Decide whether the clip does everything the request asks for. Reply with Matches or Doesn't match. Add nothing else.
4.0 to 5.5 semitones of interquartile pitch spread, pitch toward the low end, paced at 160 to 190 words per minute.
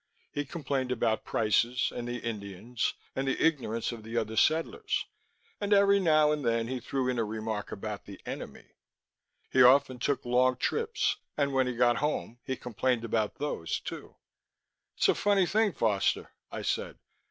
Matches